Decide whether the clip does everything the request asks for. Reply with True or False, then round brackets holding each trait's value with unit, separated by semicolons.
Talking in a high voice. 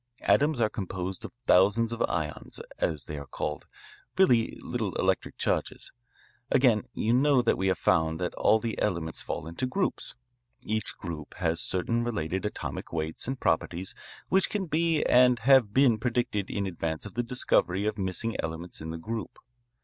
False (105 Hz)